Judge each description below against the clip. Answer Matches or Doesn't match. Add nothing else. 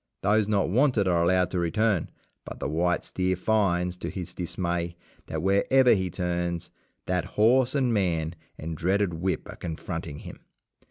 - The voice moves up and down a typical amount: Matches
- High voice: Doesn't match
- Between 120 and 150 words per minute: Doesn't match